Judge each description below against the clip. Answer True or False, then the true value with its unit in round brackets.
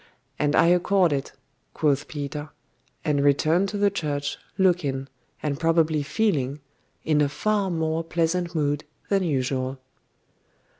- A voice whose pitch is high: False (155 Hz)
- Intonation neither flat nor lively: True (3.5 semitones)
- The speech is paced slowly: True (130 wpm)